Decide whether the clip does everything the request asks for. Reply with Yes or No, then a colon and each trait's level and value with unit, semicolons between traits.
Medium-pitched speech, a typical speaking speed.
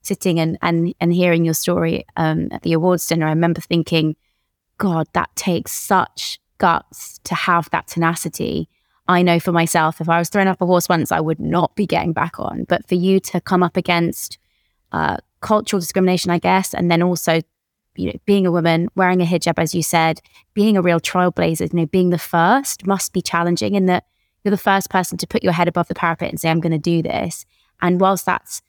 No: medium, 175 Hz; fast, 220 wpm